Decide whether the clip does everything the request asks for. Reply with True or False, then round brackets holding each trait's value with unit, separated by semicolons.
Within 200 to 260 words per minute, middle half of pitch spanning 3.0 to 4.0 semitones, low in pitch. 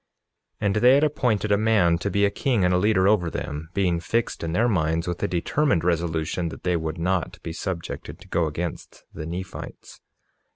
True (205 wpm; 3.7 semitones; 90 Hz)